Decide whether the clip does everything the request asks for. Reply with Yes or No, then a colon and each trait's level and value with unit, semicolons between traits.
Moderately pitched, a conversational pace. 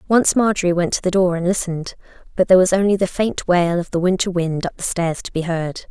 No: medium, 180 Hz; fast, 255 wpm